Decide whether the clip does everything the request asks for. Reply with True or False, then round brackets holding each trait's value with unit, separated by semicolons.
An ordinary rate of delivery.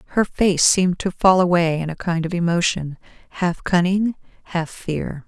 True (170 wpm)